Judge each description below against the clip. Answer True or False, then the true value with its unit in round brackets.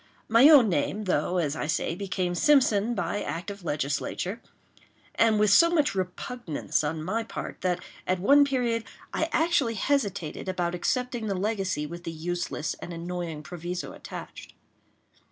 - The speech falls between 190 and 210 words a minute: False (155 wpm)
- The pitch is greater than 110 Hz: True (190 Hz)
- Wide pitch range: False (4.9 semitones)